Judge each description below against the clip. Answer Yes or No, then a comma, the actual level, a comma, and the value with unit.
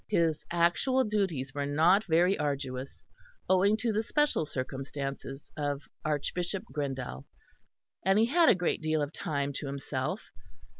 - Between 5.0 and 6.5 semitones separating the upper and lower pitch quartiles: Yes, wide, 5.5 semitones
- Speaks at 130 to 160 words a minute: Yes, average, 140 wpm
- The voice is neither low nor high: Yes, medium, 155 Hz